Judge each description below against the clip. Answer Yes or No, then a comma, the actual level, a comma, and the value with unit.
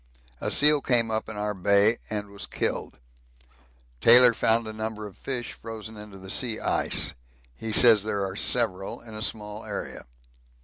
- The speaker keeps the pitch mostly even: Yes, narrow, 1.8 semitones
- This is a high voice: No, low, 110 Hz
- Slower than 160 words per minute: No, average, 170 wpm